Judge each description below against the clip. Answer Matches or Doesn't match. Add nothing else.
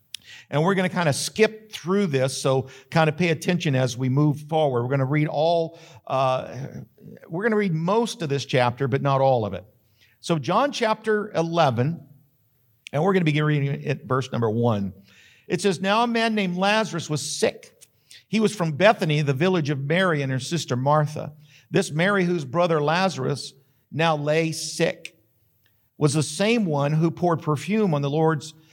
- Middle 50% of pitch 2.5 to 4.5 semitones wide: Doesn't match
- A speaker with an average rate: Matches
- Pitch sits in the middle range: Matches